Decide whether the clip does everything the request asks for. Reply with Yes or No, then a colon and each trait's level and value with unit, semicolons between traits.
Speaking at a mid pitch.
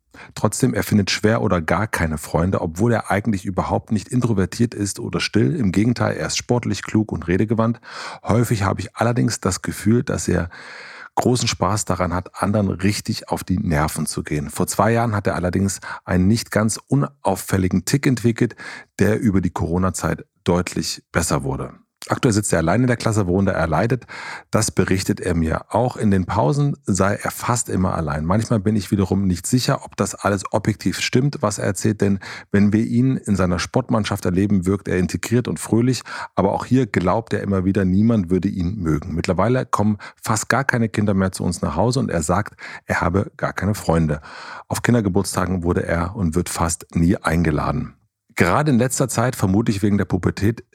No: low, 100 Hz